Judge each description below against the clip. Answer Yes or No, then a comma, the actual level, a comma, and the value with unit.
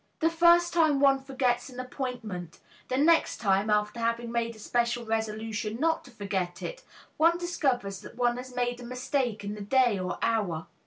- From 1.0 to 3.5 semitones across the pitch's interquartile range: No, average, 4.1 semitones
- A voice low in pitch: No, high, 240 Hz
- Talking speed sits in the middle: Yes, average, 180 wpm